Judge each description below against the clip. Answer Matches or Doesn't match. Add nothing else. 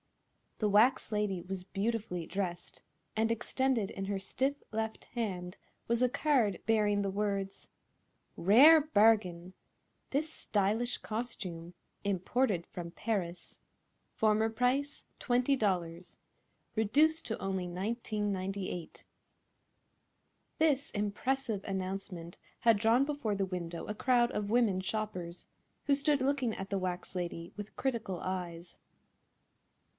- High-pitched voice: Matches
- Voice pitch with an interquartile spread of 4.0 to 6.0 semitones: Matches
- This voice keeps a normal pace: Doesn't match